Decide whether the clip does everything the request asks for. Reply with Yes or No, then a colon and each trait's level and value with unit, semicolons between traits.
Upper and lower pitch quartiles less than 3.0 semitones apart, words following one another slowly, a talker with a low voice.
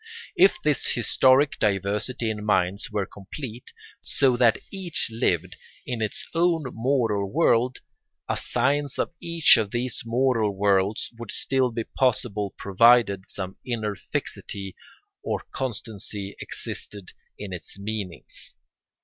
No: average, 4.3 semitones; slow, 125 wpm; low, 110 Hz